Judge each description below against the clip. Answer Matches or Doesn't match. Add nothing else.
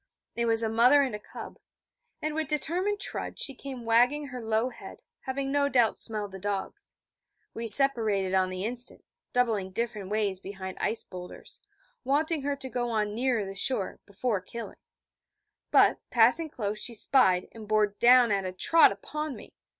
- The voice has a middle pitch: Doesn't match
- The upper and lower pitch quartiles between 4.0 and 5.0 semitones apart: Matches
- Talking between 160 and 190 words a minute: Matches